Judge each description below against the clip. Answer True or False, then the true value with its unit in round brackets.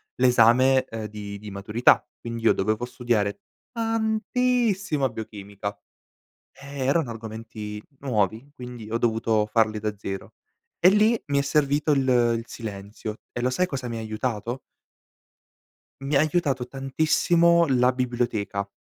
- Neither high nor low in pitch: False (120 Hz)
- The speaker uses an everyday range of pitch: True (4.6 semitones)